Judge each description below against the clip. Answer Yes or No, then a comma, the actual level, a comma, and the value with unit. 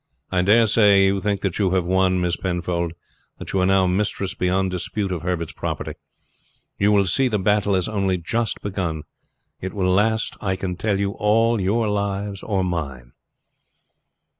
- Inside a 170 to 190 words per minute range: Yes, average, 175 wpm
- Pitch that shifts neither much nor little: No, narrow, 2.2 semitones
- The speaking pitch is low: Yes, very low, 95 Hz